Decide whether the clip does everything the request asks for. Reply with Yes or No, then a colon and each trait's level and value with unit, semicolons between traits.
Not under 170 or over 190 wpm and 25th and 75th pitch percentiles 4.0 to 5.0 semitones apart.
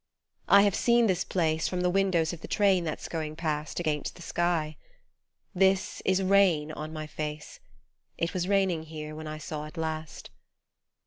No: average, 175 wpm; average, 3.3 semitones